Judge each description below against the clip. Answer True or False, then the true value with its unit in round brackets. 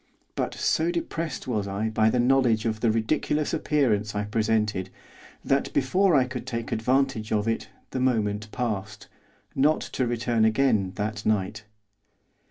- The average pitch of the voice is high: False (115 Hz)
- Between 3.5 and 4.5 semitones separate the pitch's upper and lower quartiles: True (3.8 semitones)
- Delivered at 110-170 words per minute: True (150 wpm)